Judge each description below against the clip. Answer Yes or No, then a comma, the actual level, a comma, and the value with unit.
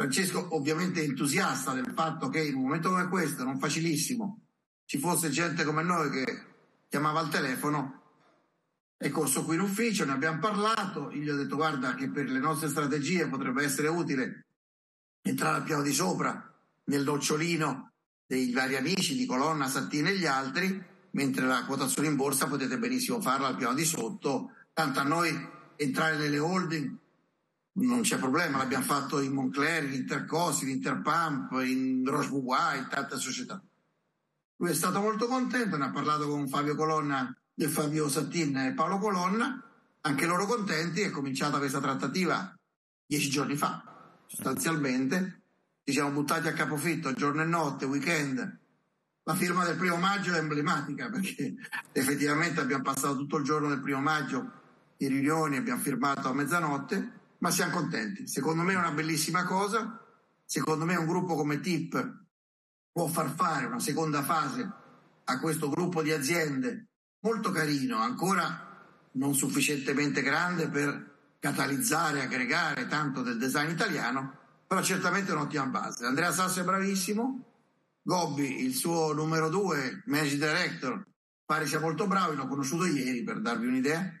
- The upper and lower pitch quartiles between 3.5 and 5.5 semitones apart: Yes, average, 4.0 semitones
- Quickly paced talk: No, average, 155 wpm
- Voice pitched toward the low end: No, medium, 155 Hz